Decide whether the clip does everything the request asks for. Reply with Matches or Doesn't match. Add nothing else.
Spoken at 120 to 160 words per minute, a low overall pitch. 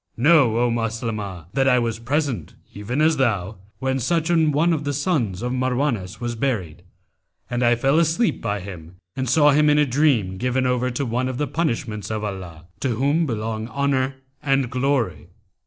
Doesn't match